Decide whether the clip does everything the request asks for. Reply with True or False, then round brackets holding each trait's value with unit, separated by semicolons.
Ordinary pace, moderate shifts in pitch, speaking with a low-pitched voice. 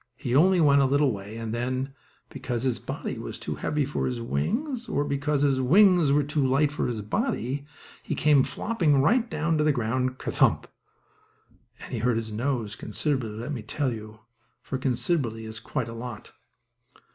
True (185 wpm; 4.4 semitones; 130 Hz)